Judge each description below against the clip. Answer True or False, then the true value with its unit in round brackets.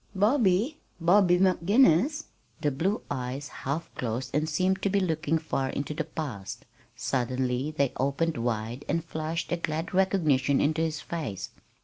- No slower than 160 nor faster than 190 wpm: False (145 wpm)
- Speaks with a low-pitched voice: False (155 Hz)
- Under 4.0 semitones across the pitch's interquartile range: False (5.3 semitones)